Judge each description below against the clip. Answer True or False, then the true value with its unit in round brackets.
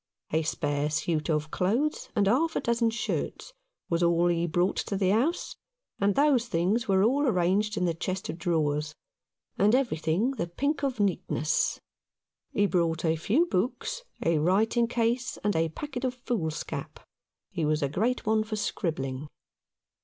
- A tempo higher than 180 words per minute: False (160 wpm)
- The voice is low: False (190 Hz)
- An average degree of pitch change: False (6.4 semitones)